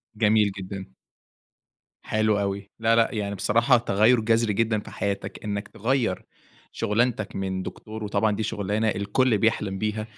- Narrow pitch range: Yes, narrow, 2.0 semitones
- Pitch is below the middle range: Yes, low, 105 Hz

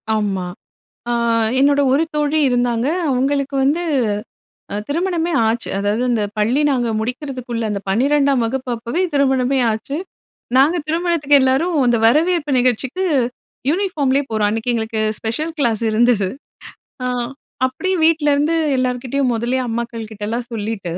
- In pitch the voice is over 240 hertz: Yes, very high, 255 Hz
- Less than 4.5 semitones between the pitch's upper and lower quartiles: Yes, average, 4.1 semitones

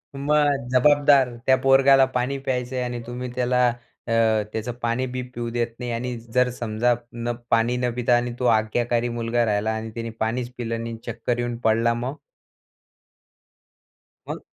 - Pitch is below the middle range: Yes, low, 120 Hz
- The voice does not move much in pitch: Yes, narrow, 1.5 semitones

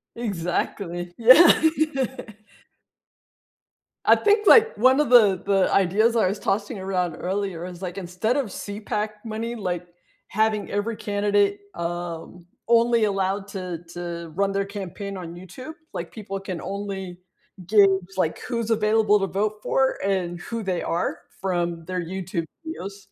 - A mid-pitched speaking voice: No, high, 195 Hz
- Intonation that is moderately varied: Yes, average, 3.3 semitones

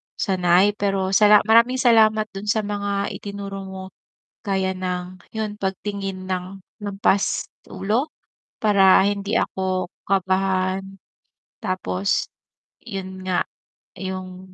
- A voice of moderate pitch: No, high, 195 Hz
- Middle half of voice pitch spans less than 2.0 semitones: Yes, narrow, 1.6 semitones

